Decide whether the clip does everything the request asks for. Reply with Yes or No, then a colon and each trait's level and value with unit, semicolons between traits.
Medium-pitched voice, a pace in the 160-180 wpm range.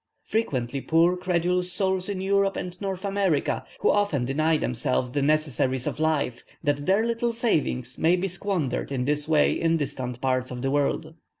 Yes: medium, 160 Hz; average, 175 wpm